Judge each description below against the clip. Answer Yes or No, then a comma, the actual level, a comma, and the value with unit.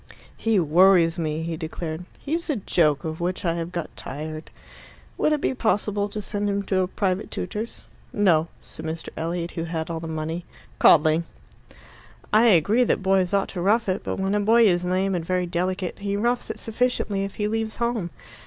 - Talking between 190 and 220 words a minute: Yes, average, 195 wpm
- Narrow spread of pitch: No, average, 3.9 semitones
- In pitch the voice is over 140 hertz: Yes, medium, 185 Hz